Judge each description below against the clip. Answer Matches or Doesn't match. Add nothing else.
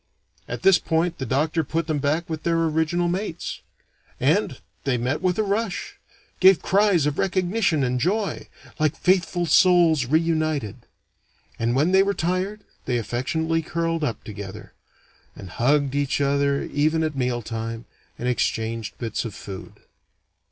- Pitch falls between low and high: Matches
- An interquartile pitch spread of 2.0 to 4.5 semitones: Doesn't match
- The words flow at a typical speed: Matches